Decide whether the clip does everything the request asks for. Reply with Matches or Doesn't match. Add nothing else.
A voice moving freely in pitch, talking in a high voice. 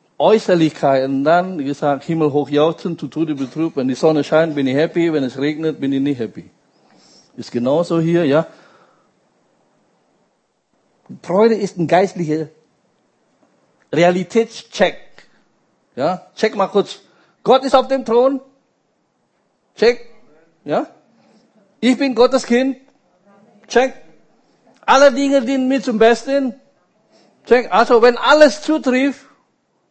Matches